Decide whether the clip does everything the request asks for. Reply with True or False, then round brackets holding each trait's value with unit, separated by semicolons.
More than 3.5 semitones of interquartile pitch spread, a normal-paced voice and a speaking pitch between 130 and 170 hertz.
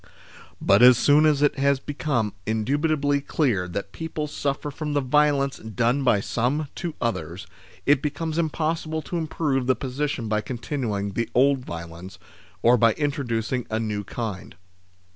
True (4.9 semitones; 155 wpm; 135 Hz)